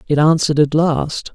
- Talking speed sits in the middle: Yes, average, 180 wpm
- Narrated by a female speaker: No, male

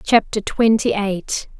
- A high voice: Yes, high, 215 Hz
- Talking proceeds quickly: No, slow, 115 wpm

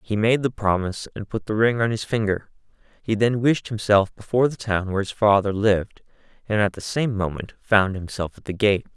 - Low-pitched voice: Yes, low, 105 Hz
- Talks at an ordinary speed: No, fast, 215 wpm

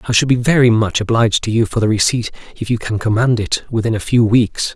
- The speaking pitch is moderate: No, low, 115 Hz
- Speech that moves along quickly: Yes, fast, 250 wpm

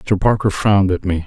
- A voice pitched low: Yes, very low, 95 Hz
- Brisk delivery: Yes, fast, 240 wpm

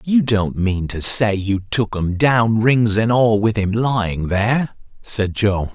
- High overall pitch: No, low, 110 Hz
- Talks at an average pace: Yes, average, 190 wpm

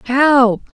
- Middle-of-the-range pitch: No, very high, 255 Hz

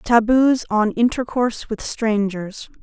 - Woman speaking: Yes, female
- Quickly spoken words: No, slow, 105 wpm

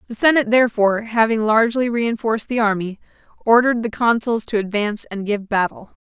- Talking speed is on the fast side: No, average, 160 wpm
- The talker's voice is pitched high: Yes, high, 225 Hz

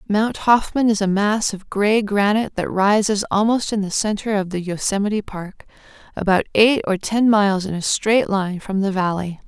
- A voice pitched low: No, high, 205 Hz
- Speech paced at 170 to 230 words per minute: Yes, average, 190 wpm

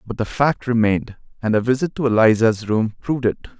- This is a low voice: Yes, low, 115 Hz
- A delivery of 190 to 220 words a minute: Yes, average, 200 wpm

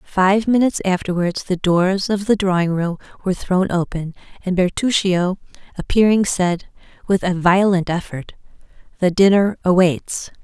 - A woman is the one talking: Yes, female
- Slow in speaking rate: Yes, slow, 130 wpm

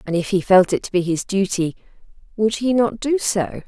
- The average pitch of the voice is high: Yes, high, 200 Hz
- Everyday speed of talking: No, fast, 230 wpm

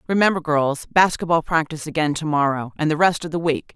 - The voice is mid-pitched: Yes, medium, 160 Hz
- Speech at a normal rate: No, fast, 210 wpm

